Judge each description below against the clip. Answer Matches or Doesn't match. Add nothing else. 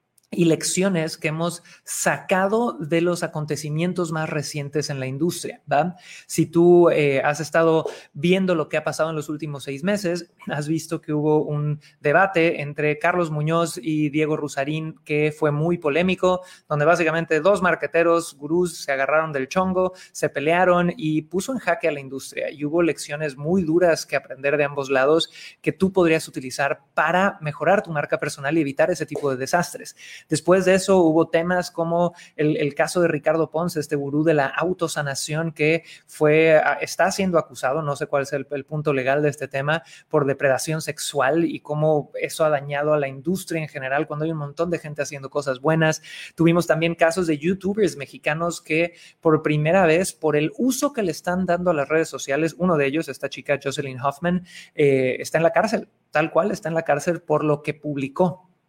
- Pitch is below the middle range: Doesn't match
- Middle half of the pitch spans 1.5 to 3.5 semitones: Matches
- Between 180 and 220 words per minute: Matches